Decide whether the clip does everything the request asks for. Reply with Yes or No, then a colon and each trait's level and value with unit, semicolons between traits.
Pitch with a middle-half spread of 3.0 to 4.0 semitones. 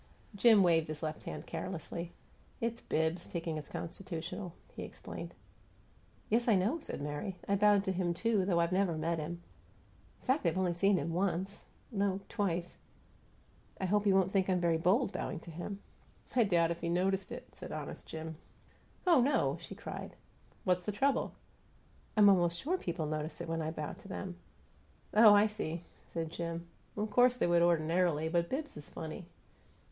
Yes: average, 3.4 semitones